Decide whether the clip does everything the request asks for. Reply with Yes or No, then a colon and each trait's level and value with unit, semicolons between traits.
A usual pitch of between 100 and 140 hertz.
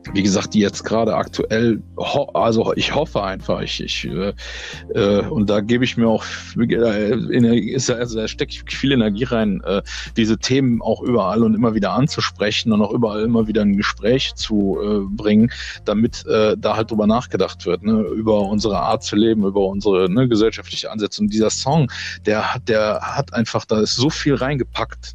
Yes: low, 110 Hz